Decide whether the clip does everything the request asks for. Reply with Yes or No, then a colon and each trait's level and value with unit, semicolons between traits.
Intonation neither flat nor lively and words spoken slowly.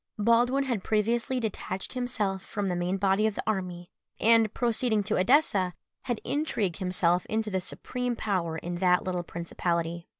No: average, 4.3 semitones; average, 160 wpm